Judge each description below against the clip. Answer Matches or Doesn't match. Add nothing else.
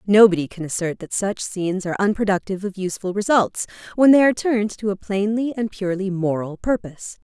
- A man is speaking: Doesn't match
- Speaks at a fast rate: Doesn't match